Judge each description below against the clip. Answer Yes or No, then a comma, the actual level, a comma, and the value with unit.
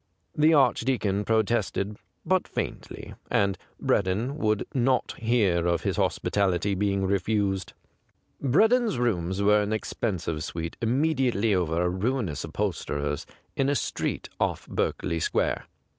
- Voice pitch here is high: No, low, 105 Hz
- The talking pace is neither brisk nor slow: No, slow, 130 wpm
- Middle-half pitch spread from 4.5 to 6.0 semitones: Yes, average, 4.8 semitones